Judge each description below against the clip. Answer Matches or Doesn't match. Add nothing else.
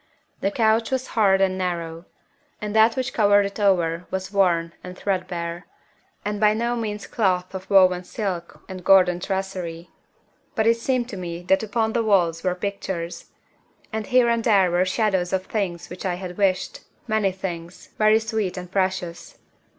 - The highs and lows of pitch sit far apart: Doesn't match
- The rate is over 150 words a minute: Matches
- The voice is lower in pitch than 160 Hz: Doesn't match